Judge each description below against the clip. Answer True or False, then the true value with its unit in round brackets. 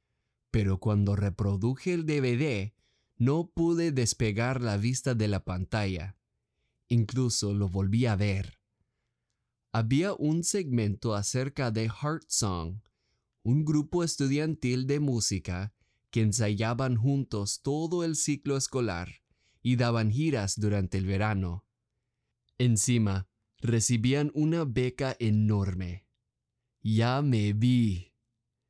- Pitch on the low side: True (115 Hz)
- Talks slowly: True (105 wpm)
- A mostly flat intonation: False (4.3 semitones)